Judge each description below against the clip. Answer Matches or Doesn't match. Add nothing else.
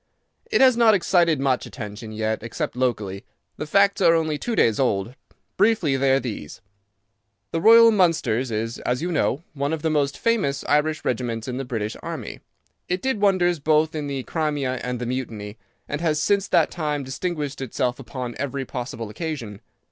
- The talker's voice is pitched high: Doesn't match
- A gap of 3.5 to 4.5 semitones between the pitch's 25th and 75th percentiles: Doesn't match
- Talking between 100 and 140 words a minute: Doesn't match